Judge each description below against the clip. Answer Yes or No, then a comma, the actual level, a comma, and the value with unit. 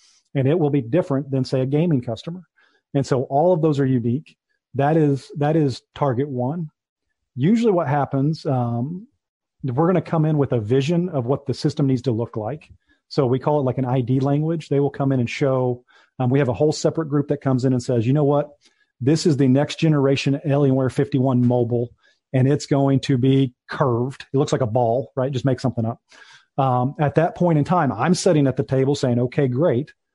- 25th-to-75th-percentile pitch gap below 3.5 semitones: Yes, average, 2.7 semitones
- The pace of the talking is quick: Yes, fast, 220 wpm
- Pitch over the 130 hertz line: Yes, medium, 140 Hz